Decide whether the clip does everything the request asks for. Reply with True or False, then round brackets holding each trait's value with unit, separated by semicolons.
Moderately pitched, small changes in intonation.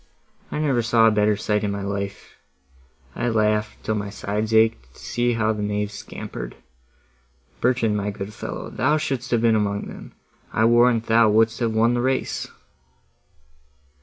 False (110 Hz; 2.2 semitones)